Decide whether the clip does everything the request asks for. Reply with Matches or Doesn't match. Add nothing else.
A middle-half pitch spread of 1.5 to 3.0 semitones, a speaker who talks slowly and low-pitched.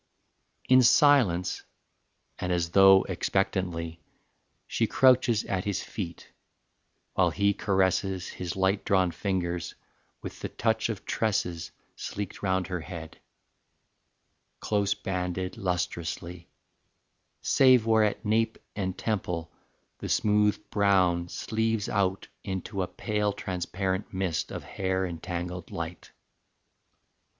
Matches